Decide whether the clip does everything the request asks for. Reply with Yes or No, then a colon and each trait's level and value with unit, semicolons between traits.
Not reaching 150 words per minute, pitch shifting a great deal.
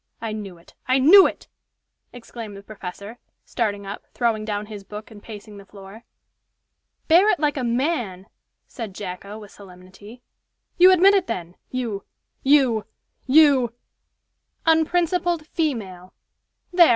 Yes: average, 140 wpm; wide, 6.6 semitones